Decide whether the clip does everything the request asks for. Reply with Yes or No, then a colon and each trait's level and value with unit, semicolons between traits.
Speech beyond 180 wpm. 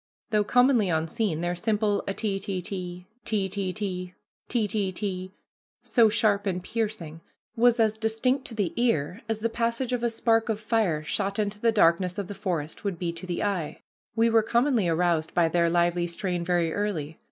Yes: average, 190 wpm